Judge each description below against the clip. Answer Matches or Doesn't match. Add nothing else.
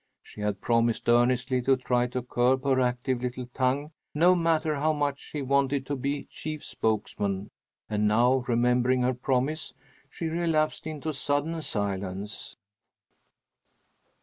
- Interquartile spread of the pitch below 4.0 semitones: Matches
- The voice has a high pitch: Doesn't match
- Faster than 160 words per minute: Doesn't match